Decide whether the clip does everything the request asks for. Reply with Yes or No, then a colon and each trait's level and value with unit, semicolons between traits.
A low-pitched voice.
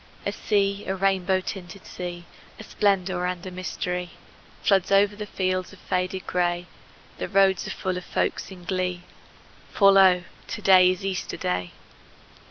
No: medium, 185 Hz